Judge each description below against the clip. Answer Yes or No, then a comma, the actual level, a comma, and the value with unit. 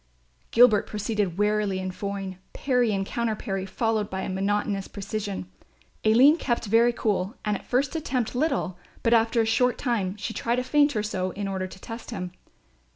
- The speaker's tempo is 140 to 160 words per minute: No, average, 170 wpm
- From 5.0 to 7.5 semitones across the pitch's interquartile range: No, average, 3.4 semitones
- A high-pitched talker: Yes, high, 215 Hz